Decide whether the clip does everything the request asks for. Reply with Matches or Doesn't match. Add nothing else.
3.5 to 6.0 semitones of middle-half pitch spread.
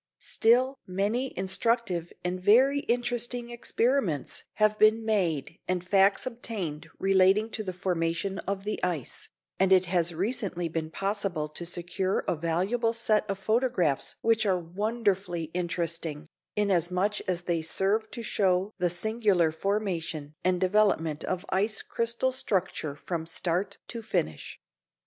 Matches